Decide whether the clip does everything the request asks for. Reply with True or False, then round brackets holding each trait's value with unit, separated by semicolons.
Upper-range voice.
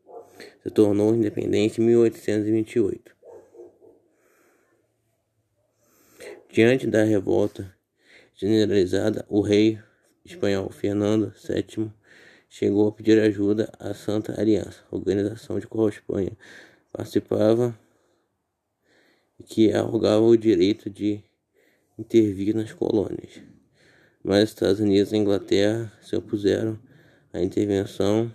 False (110 Hz)